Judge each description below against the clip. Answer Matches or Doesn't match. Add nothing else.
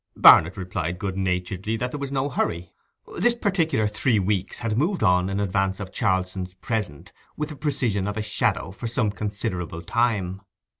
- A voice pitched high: Doesn't match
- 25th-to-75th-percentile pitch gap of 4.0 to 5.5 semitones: Matches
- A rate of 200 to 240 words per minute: Doesn't match